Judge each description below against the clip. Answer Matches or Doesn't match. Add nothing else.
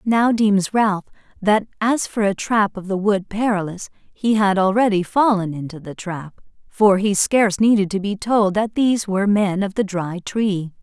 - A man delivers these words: Doesn't match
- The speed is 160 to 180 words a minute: Doesn't match